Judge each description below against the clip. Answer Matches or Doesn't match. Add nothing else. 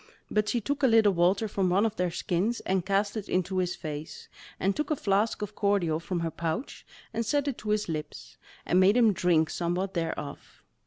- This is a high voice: Matches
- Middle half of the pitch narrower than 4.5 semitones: Matches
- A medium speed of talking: Doesn't match